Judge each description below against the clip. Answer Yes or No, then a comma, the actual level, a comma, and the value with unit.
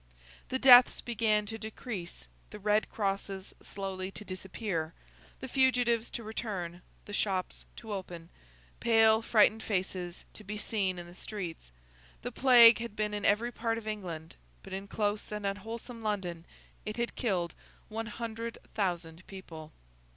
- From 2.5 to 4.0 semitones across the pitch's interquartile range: Yes, average, 3.3 semitones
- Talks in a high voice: Yes, high, 210 Hz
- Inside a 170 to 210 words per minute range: No, average, 150 wpm